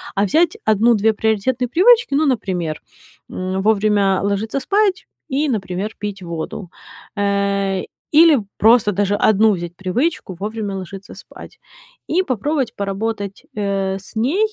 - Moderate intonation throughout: Yes, average, 4.6 semitones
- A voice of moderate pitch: No, high, 210 Hz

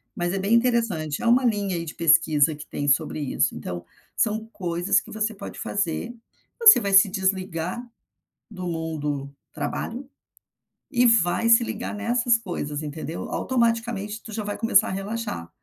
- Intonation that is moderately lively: No, wide, 5.9 semitones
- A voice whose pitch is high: Yes, high, 195 Hz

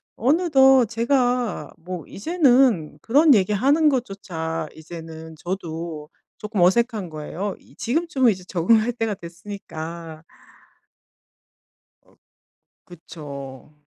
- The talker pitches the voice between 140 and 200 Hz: Yes, high, 195 Hz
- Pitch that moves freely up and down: Yes, wide, 7.2 semitones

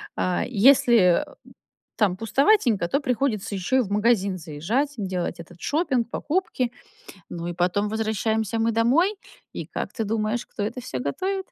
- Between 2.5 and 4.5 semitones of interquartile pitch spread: No, average, 5.1 semitones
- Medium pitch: No, high, 220 Hz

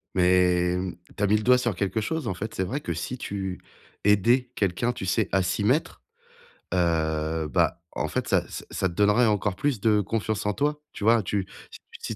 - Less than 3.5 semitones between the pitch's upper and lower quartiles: No, average, 4.0 semitones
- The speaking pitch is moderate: No, low, 100 Hz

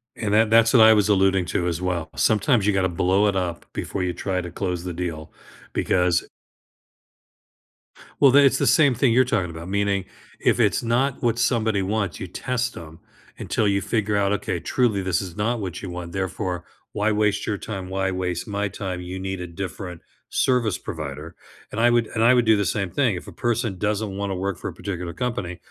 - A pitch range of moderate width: Yes, average, 3.6 semitones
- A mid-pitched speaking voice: No, low, 100 Hz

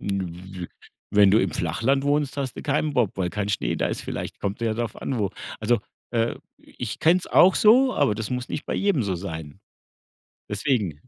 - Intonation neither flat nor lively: No, wide, 5.9 semitones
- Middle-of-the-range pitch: No, low, 110 Hz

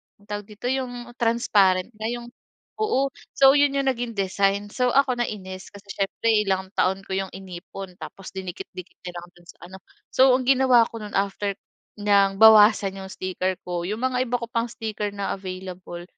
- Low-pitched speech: No, high, 205 Hz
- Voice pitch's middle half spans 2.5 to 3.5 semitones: No, average, 4.0 semitones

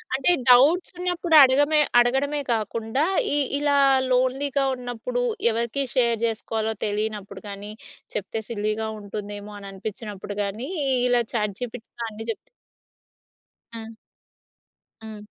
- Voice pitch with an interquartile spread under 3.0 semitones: No, average, 3.7 semitones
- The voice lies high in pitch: Yes, high, 230 Hz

